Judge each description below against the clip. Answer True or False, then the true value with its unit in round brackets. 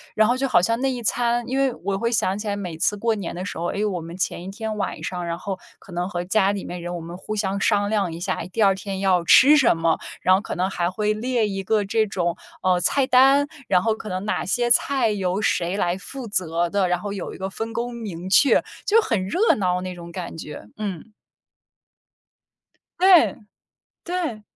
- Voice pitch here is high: True (200 Hz)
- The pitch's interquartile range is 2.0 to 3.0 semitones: False (4.0 semitones)